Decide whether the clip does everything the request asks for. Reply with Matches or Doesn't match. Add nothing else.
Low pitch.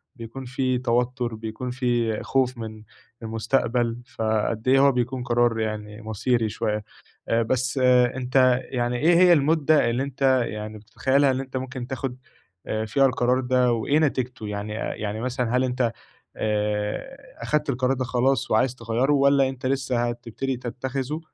Matches